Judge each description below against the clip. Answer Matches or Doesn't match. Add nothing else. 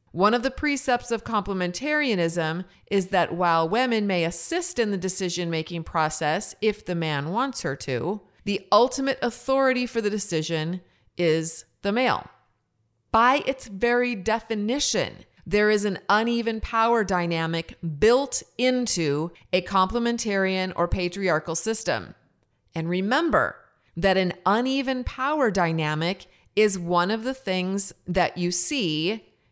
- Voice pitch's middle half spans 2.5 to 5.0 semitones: Doesn't match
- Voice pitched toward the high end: Matches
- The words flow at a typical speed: Doesn't match